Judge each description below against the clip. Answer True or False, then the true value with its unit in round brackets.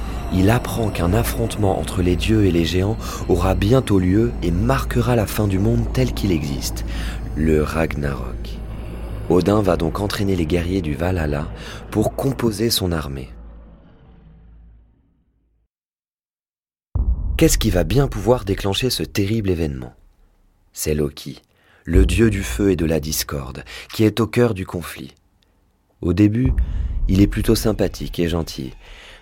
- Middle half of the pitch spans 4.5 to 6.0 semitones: True (4.8 semitones)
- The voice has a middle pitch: False (95 Hz)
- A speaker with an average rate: False (140 wpm)